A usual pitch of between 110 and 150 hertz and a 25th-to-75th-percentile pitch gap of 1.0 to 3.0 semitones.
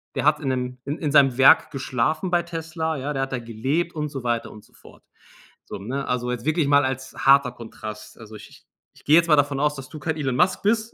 No: medium, 140 Hz; average, 3.7 semitones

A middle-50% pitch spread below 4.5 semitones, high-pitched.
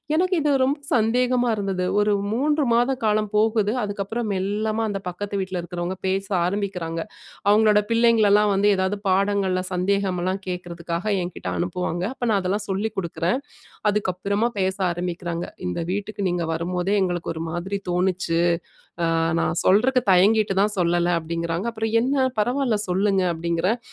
Yes: average, 3.3 semitones; high, 195 Hz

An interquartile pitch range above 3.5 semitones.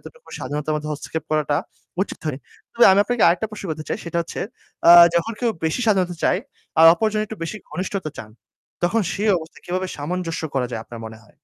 Yes: average, 5.0 semitones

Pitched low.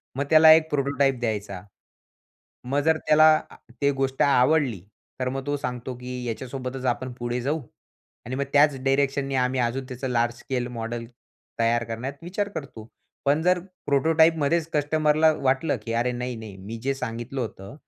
Yes: low, 130 Hz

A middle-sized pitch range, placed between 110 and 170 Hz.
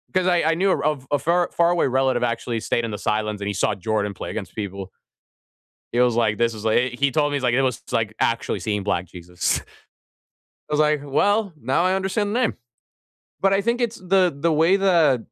No: wide, 8.3 semitones; low, 135 Hz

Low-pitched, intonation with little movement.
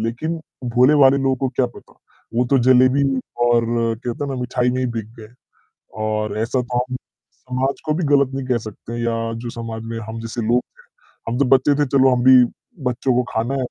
Yes: low, 125 Hz; narrow, 2.3 semitones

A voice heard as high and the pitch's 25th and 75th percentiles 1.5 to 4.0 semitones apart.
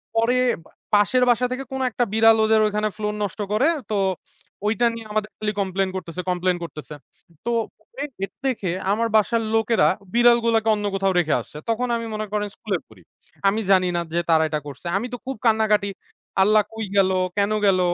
Yes: high, 215 Hz; average, 2.9 semitones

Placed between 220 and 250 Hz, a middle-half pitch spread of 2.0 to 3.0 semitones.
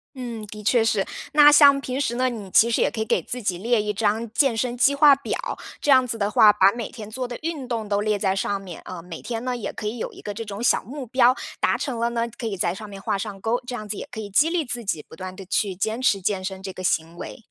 No: high, 225 Hz; average, 3.8 semitones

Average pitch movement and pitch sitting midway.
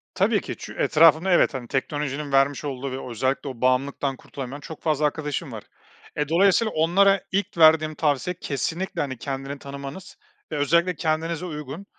Yes: average, 3.3 semitones; medium, 150 Hz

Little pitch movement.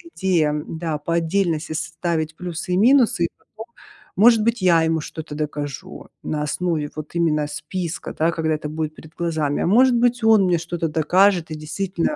No: average, 3.3 semitones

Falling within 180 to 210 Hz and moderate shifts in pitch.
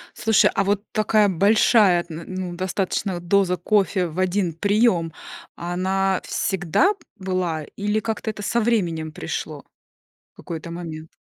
Yes: medium, 185 Hz; average, 3.1 semitones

